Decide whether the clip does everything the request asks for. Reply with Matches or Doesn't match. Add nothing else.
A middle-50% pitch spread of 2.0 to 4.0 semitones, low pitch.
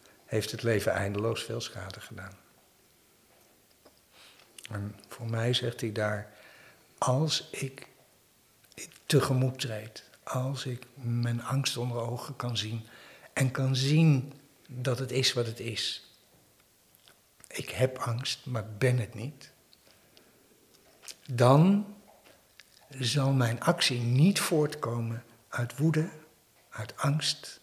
Matches